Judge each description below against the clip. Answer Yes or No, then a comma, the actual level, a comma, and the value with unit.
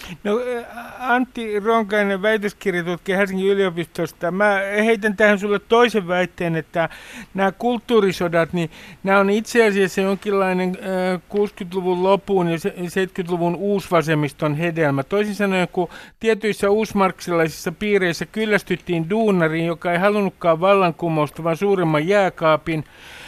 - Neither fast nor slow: Yes, average, 110 wpm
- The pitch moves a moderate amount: Yes, average, 3.1 semitones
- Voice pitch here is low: No, high, 195 Hz